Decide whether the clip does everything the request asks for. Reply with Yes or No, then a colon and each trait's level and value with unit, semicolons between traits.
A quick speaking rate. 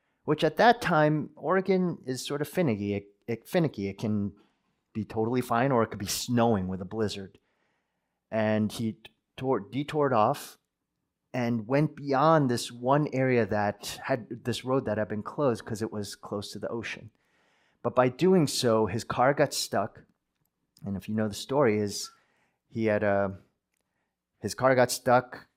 No: average, 170 wpm